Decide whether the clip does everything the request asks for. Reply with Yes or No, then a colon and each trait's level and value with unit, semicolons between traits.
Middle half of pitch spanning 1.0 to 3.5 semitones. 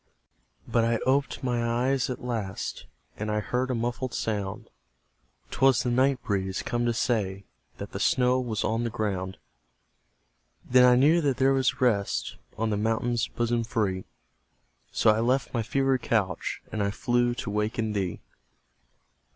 Yes: average, 2.8 semitones